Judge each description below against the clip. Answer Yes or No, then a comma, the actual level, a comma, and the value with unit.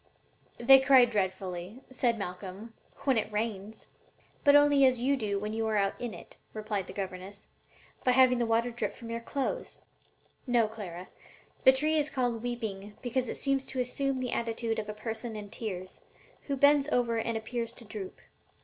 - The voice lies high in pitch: Yes, high, 230 Hz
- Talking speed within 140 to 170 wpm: No, average, 180 wpm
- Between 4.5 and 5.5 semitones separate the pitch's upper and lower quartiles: No, average, 3.6 semitones